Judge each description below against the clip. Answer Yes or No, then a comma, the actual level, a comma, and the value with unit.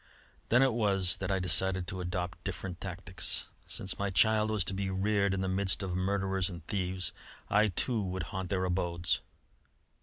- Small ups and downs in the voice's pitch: Yes, narrow, 1.7 semitones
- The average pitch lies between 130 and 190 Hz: No, very low, 95 Hz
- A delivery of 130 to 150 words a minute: No, average, 180 wpm